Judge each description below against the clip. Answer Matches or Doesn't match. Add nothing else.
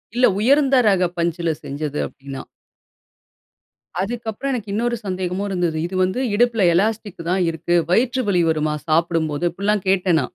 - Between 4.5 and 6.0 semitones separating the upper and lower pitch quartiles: Matches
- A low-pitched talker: Doesn't match